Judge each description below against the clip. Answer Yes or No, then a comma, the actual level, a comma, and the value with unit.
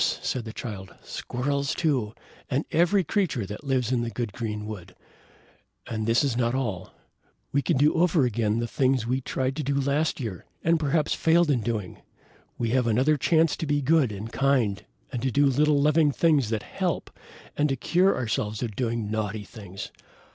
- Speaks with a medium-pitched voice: No, low, 130 Hz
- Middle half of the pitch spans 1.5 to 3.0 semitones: No, average, 4.8 semitones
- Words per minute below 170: No, average, 185 wpm